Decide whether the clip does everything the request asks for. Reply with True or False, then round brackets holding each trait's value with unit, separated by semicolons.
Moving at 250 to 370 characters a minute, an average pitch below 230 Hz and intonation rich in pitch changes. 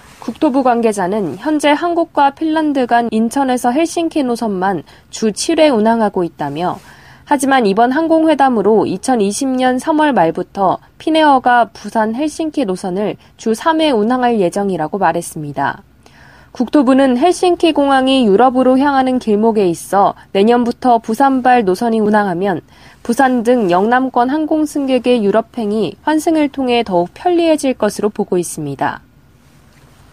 False (295 characters per minute; 245 Hz; 5.7 semitones)